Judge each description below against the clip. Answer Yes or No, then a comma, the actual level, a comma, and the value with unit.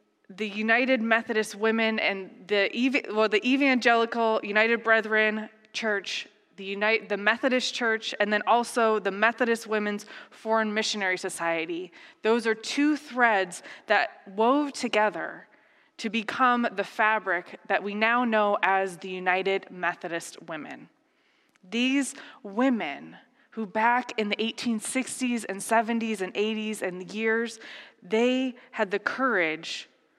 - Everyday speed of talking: No, slow, 125 wpm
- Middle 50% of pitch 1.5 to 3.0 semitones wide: Yes, narrow, 2.5 semitones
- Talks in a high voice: Yes, high, 220 Hz